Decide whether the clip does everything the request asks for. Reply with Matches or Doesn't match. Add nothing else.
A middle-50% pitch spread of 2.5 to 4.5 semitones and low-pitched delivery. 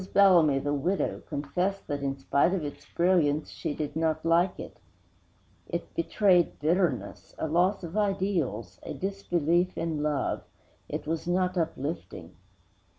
Doesn't match